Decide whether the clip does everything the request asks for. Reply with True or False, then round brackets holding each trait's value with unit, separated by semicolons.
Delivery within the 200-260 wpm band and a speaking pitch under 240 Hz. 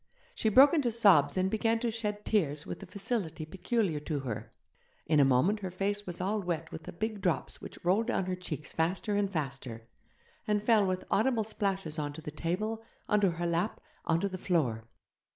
True (205 wpm; 185 Hz)